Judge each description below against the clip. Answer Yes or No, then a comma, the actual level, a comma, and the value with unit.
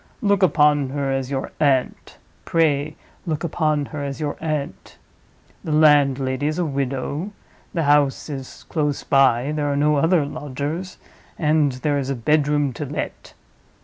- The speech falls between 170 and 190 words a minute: No, average, 150 wpm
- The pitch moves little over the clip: Yes, narrow, 1.9 semitones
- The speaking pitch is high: No, medium, 145 Hz